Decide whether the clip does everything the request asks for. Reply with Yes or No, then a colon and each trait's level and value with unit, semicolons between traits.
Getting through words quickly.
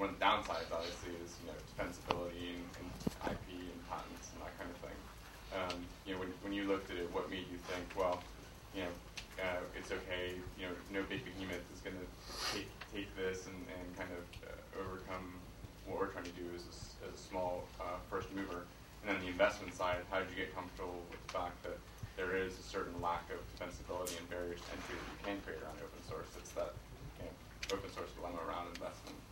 Yes: fast, 220 wpm